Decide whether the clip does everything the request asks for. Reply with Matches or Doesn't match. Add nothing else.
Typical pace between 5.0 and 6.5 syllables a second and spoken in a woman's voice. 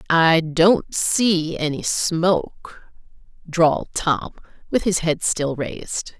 Doesn't match